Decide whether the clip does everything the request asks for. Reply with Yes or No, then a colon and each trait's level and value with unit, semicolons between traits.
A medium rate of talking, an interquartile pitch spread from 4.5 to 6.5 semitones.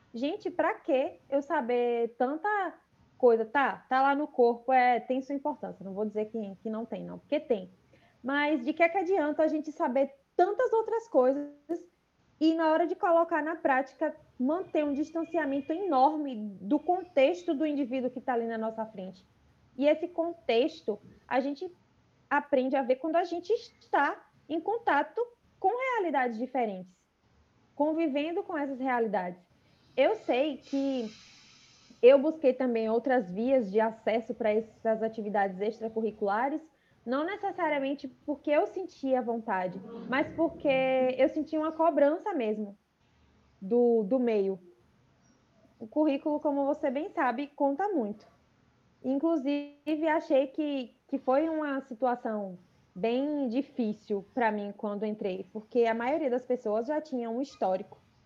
Yes: average, 145 wpm; average, 5.2 semitones